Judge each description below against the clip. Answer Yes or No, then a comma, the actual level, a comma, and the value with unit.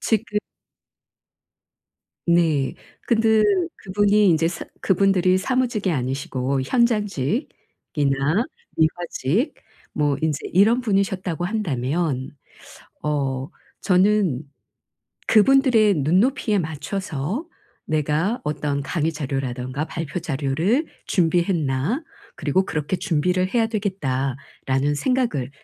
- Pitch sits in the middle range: Yes, medium, 170 Hz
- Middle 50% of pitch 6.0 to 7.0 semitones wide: Yes, wide, 6.6 semitones